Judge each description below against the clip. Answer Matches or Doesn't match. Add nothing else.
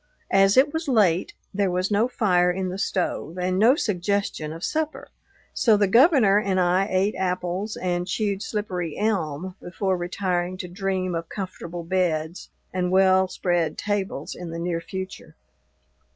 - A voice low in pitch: Doesn't match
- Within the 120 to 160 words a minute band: Matches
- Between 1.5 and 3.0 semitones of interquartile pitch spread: Matches